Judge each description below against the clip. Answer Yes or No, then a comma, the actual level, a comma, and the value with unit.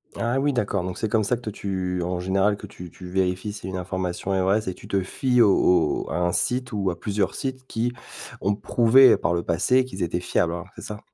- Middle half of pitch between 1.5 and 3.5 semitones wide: No, average, 3.9 semitones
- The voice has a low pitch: Yes, very low, 95 Hz